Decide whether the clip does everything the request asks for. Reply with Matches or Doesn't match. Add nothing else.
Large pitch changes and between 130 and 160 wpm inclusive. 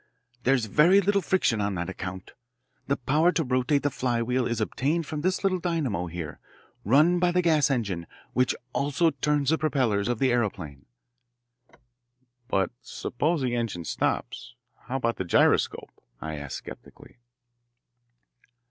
Matches